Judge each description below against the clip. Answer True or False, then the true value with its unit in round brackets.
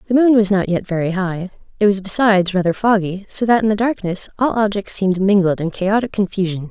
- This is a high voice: True (200 Hz)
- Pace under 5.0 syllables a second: False (5.9 syllables/s)